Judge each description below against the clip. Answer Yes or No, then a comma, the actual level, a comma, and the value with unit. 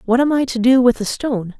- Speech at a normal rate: No, fast, 300 wpm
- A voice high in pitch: Yes, high, 245 Hz